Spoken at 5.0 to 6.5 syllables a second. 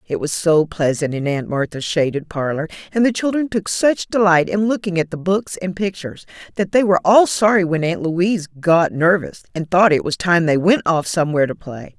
Yes: 5.3 syllables/s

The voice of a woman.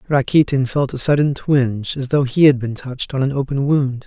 No: male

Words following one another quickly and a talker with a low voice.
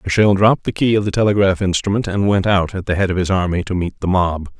Yes: fast, 275 wpm; very low, 95 Hz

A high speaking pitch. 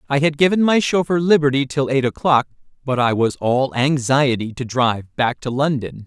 No: medium, 140 Hz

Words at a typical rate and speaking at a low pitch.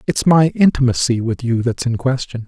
Yes: average, 195 wpm; low, 125 Hz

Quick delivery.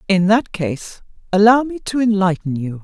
No: average, 170 wpm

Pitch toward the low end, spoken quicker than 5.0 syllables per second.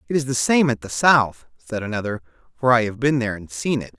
Yes: low, 120 Hz; 6.0 syllables/s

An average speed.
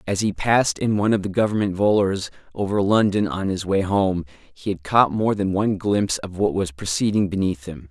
No: fast, 210 wpm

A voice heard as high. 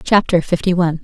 No: medium, 175 Hz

